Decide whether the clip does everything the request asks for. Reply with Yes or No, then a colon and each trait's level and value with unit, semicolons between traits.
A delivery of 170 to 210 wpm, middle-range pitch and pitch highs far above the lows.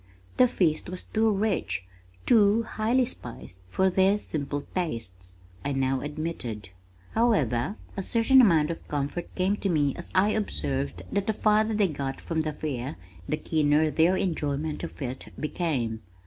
No: average, 155 wpm; medium, 160 Hz; wide, 6.9 semitones